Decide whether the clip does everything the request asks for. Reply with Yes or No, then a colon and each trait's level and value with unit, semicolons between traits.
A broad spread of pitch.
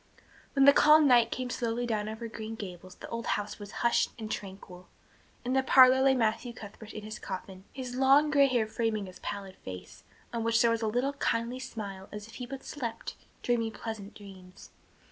No: average, 3.5 semitones